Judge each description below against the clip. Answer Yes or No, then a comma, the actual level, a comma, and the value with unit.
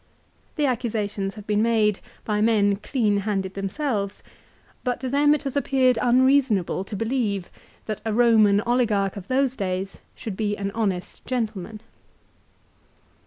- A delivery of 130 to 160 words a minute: Yes, average, 140 wpm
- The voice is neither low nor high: No, high, 215 Hz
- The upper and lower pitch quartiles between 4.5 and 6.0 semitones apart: No, average, 3.8 semitones